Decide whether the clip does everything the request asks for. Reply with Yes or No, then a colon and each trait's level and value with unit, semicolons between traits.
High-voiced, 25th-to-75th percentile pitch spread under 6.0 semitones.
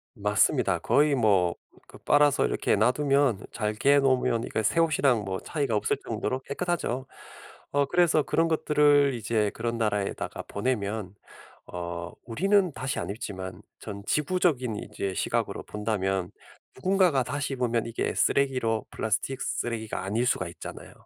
No: low, 120 Hz; average, 5.3 semitones